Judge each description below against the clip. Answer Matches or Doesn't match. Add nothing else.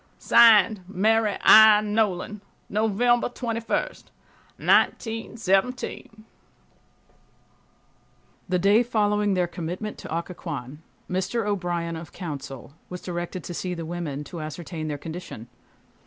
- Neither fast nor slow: Doesn't match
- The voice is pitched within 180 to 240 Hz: Matches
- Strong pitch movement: Doesn't match